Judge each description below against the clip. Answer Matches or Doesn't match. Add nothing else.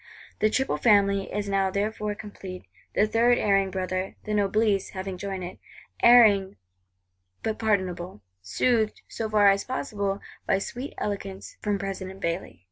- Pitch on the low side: Doesn't match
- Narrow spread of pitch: Matches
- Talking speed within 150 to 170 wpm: Doesn't match